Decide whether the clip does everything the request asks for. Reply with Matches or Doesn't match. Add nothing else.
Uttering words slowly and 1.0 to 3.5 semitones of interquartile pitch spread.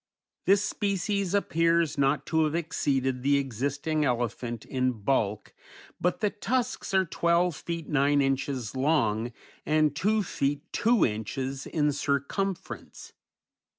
Doesn't match